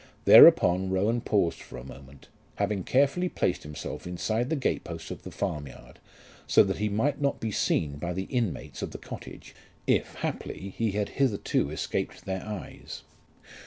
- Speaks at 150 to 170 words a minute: Yes, average, 165 wpm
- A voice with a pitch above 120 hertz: No, very low, 95 Hz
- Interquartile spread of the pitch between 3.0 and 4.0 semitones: No, average, 5.3 semitones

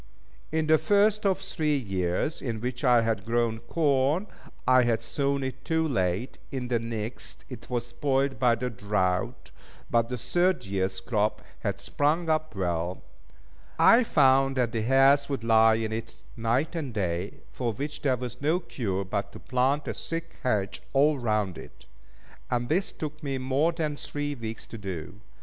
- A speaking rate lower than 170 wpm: No, average, 175 wpm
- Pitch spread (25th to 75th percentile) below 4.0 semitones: No, average, 4.8 semitones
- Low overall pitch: Yes, low, 125 Hz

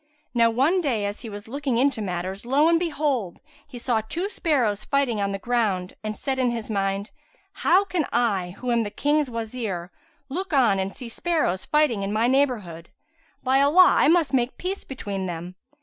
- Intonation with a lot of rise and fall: Yes, wide, 5.9 semitones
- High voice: Yes, high, 240 Hz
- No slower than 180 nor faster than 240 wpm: Yes, average, 190 wpm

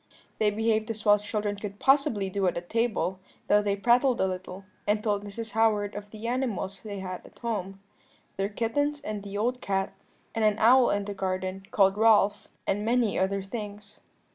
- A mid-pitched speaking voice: No, high, 205 Hz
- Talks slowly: No, average, 190 wpm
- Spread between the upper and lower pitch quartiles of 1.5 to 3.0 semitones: Yes, narrow, 2.4 semitones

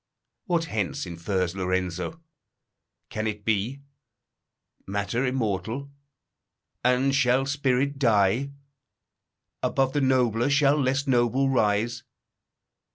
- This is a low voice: Yes, low, 125 Hz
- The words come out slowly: Yes, slow, 95 wpm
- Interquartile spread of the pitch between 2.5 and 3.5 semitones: No, average, 4.8 semitones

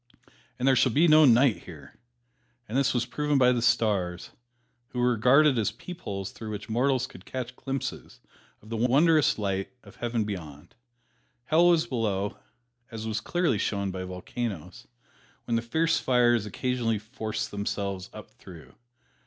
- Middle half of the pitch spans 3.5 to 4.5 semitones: Yes, average, 4.2 semitones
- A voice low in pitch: Yes, low, 115 Hz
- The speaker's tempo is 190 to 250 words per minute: No, average, 155 wpm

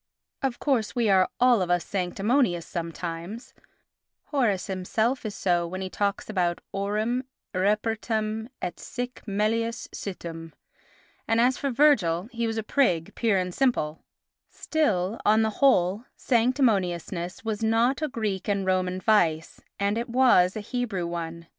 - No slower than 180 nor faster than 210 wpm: No, average, 145 wpm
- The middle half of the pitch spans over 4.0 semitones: Yes, average, 4.5 semitones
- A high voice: Yes, high, 210 Hz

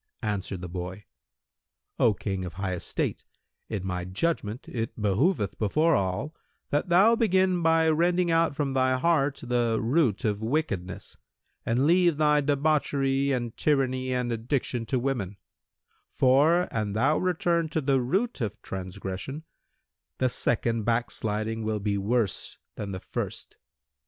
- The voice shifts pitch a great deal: Yes, wide, 6.7 semitones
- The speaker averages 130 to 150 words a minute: Yes, average, 140 wpm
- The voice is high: No, low, 125 Hz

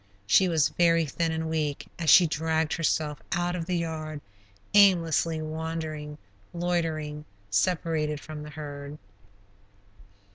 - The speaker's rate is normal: No, slow, 120 wpm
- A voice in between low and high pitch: Yes, medium, 160 Hz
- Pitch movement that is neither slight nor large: No, narrow, 1.7 semitones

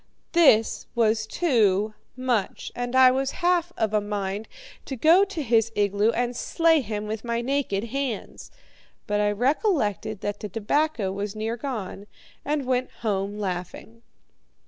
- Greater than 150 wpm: No, average, 145 wpm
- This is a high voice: Yes, high, 225 Hz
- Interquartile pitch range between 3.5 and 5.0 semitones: Yes, average, 4.5 semitones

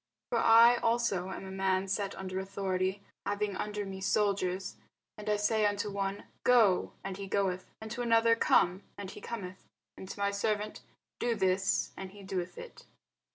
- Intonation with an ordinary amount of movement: No, narrow, 1.9 semitones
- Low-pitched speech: No, high, 200 Hz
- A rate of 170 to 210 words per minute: Yes, average, 175 wpm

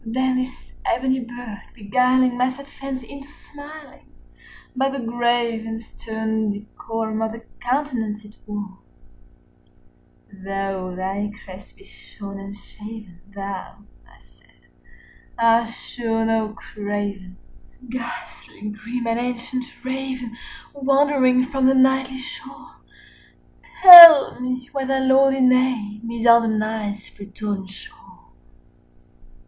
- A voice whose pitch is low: No, high, 235 Hz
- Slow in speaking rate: Yes, slow, 120 wpm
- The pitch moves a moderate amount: Yes, average, 3.6 semitones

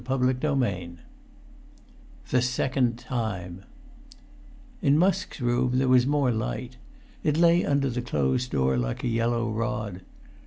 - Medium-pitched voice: No, low, 125 Hz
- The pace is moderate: No, slow, 130 wpm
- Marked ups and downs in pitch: No, average, 3.4 semitones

